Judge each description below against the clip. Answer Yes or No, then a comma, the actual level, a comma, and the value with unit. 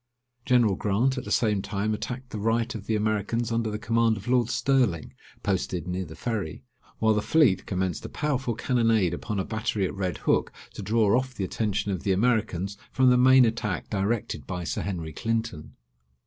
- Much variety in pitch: No, average, 3.4 semitones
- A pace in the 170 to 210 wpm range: Yes, average, 190 wpm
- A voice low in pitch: Yes, low, 110 Hz